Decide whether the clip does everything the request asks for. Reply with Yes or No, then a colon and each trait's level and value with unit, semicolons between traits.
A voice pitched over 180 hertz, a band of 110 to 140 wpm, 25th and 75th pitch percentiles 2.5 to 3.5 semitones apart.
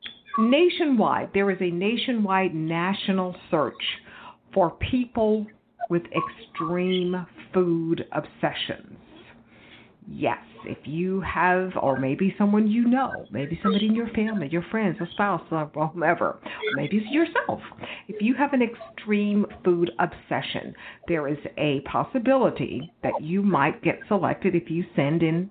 No: high, 190 Hz; slow, 135 wpm; average, 4.6 semitones